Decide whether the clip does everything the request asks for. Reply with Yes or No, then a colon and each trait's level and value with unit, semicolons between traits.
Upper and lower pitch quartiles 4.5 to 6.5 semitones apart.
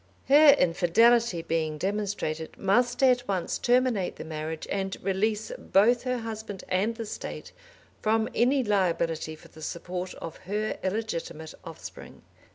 Yes: average, 5.3 semitones